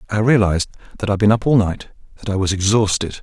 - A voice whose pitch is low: Yes, low, 105 Hz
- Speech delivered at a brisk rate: Yes, fast, 225 wpm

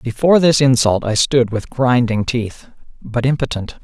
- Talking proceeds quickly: No, average, 155 wpm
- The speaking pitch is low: Yes, low, 125 Hz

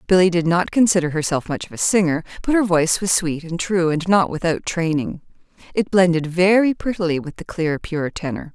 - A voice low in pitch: No, medium, 175 Hz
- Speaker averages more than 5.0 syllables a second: Yes, 5.5 syllables/s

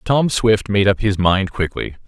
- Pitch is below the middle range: Yes, low, 105 Hz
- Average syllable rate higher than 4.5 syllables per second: No, 4.3 syllables/s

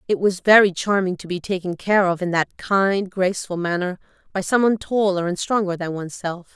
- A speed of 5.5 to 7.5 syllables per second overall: Yes, 5.6 syllables/s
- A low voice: No, high, 190 Hz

